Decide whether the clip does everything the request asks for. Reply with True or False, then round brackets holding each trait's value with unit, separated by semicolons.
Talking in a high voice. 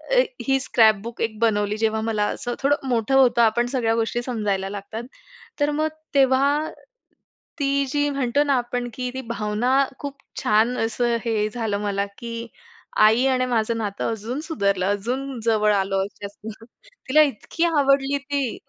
True (235 Hz)